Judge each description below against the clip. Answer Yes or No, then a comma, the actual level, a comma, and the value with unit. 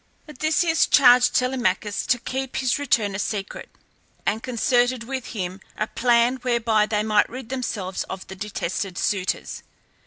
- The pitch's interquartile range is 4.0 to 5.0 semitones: No, average, 3.6 semitones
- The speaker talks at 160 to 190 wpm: No, average, 145 wpm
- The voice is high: Yes, high, 235 Hz